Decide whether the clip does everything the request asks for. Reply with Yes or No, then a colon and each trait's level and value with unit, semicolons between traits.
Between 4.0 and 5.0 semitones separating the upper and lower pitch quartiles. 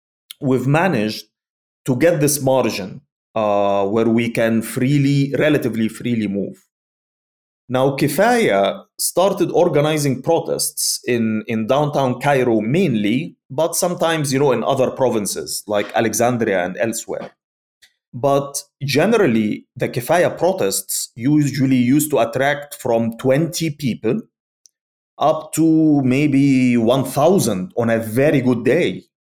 Yes: average, 4.5 semitones